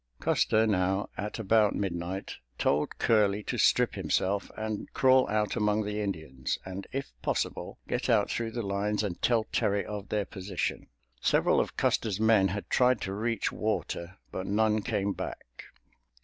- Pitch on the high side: No, low, 105 Hz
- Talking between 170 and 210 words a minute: No, average, 160 wpm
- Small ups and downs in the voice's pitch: Yes, narrow, 2.1 semitones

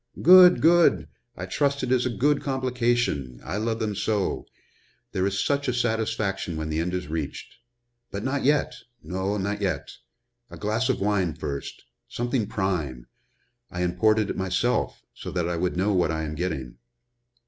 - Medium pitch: No, low, 100 Hz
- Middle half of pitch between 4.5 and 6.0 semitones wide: Yes, wide, 5.5 semitones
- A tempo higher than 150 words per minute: Yes, average, 170 wpm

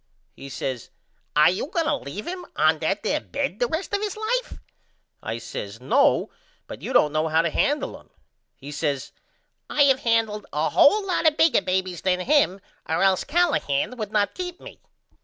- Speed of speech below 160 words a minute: No, average, 185 wpm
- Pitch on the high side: Yes, high, 210 Hz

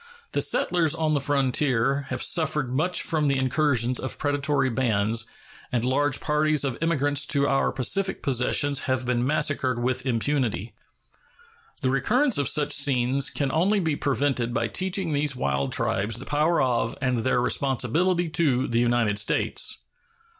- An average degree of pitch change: Yes, average, 3.3 semitones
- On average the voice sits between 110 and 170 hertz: Yes, low, 135 Hz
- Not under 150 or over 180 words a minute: Yes, average, 155 wpm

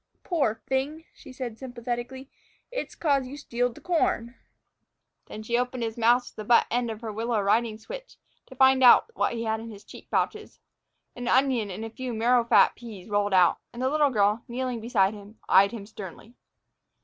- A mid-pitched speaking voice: No, high, 235 Hz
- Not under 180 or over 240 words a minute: Yes, average, 190 wpm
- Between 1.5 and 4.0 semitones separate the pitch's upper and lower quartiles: Yes, average, 3.0 semitones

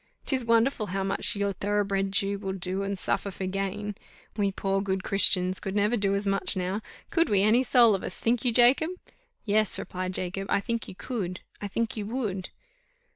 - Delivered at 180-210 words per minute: Yes, average, 195 wpm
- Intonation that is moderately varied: No, narrow, 2.3 semitones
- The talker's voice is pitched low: No, high, 200 Hz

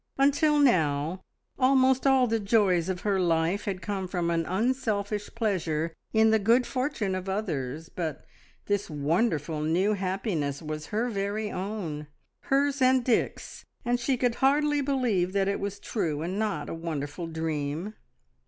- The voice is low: No, high, 200 Hz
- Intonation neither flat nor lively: No, wide, 6.3 semitones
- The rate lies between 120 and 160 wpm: Yes, average, 155 wpm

